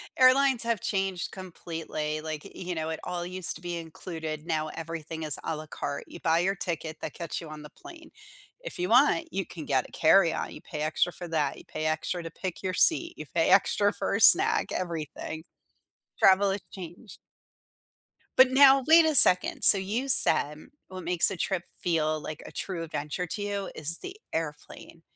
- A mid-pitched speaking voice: Yes, medium, 175 Hz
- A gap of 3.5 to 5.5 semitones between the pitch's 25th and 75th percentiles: Yes, average, 4.1 semitones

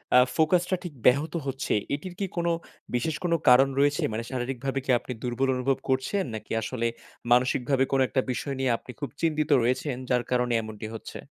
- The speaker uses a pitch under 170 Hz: Yes, low, 135 Hz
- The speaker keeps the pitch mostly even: No, average, 3.3 semitones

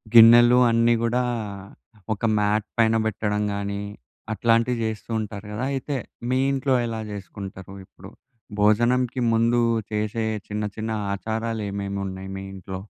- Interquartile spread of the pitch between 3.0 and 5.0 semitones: No, narrow, 2.5 semitones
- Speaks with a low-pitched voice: Yes, low, 110 Hz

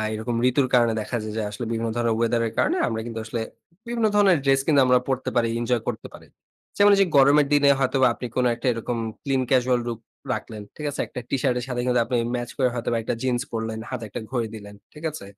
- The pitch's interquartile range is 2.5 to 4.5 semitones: Yes, average, 2.8 semitones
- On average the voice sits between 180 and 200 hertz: No, low, 125 Hz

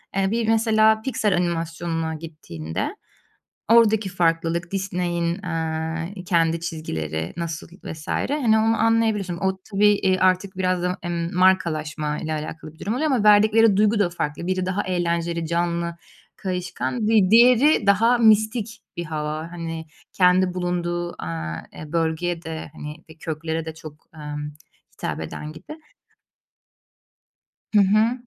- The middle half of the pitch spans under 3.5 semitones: No, average, 4.2 semitones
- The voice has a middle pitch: Yes, medium, 175 Hz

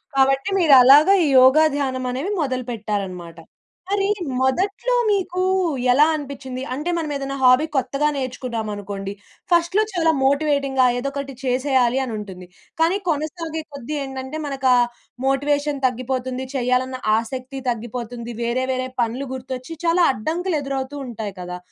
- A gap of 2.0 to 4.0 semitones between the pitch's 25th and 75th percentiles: Yes, average, 2.9 semitones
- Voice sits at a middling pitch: No, very high, 265 Hz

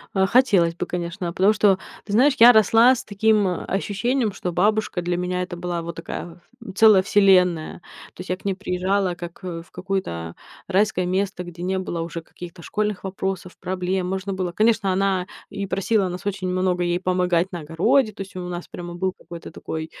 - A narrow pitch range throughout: Yes, narrow, 2.2 semitones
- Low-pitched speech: No, medium, 185 Hz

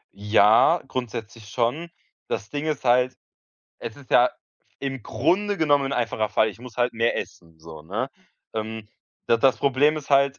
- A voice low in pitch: Yes, low, 125 Hz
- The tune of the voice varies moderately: Yes, average, 4.1 semitones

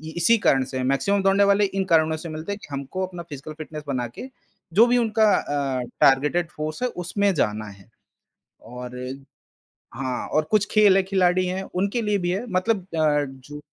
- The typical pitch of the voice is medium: Yes, medium, 170 Hz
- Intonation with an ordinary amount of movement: No, wide, 6.3 semitones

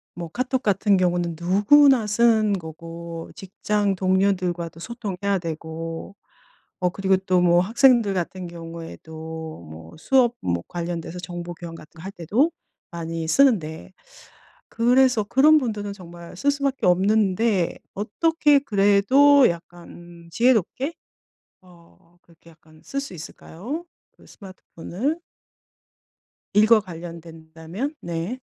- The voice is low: No, medium, 185 Hz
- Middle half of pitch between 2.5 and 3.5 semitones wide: No, average, 5.3 semitones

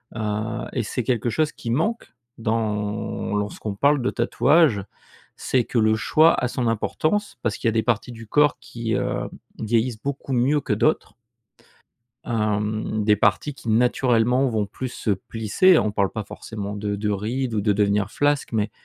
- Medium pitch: No, low, 115 Hz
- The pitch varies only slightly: No, average, 3.3 semitones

